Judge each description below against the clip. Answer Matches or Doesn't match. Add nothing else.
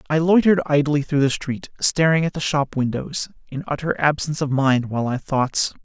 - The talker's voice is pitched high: Doesn't match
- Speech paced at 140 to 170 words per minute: Doesn't match